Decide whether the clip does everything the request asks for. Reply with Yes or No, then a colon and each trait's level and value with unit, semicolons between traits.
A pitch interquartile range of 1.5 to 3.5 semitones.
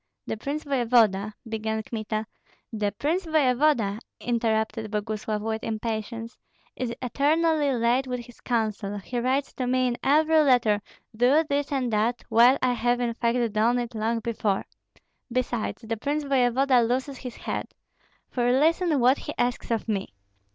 Yes: average, 3.2 semitones